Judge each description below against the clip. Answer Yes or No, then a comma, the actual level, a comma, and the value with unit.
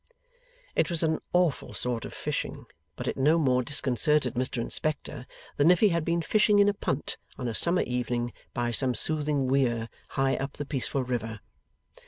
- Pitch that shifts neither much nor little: Yes, average, 4.3 semitones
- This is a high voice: No, low, 135 Hz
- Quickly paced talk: No, average, 180 wpm